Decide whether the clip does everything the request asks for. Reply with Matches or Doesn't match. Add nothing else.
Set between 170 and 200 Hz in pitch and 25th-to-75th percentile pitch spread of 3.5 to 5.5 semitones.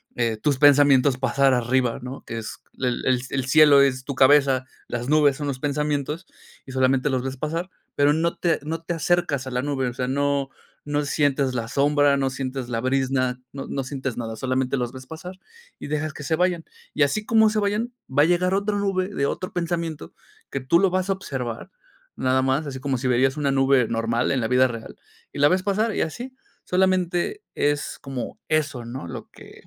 Doesn't match